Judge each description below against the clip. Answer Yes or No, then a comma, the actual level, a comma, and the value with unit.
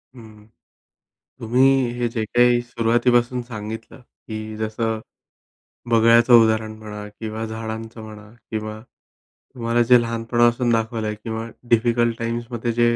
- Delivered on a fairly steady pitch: Yes, narrow, 1.3 semitones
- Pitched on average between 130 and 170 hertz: No, low, 115 Hz